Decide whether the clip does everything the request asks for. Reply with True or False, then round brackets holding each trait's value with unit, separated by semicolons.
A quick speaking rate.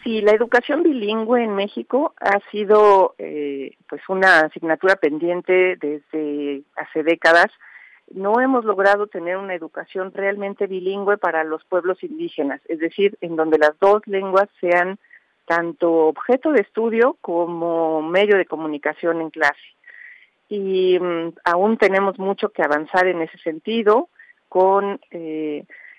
False (130 wpm)